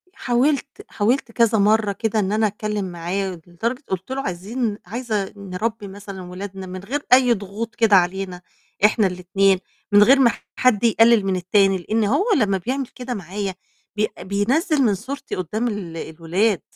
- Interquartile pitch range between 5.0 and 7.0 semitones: No, average, 3.6 semitones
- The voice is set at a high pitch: Yes, high, 205 Hz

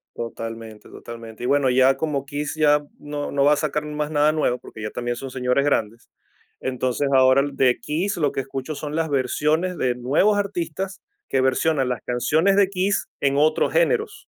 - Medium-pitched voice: Yes, medium, 145 Hz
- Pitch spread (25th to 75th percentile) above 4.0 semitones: No, average, 3.7 semitones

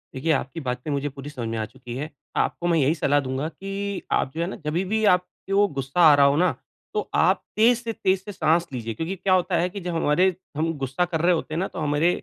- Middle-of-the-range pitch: Yes, medium, 165 Hz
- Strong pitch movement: No, average, 4.7 semitones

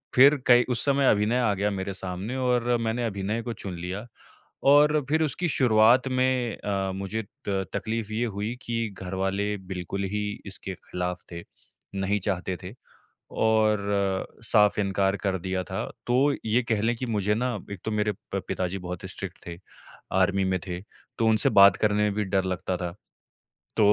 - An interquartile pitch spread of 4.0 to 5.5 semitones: No, average, 3.3 semitones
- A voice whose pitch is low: Yes, low, 105 Hz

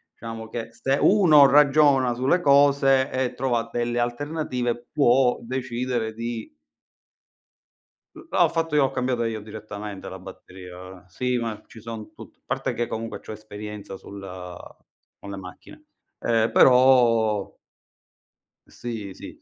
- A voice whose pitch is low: Yes, low, 120 Hz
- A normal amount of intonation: Yes, average, 3.4 semitones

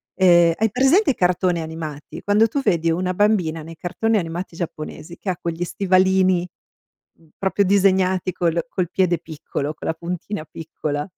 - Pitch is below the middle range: No, medium, 180 Hz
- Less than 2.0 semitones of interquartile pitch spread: No, narrow, 2.5 semitones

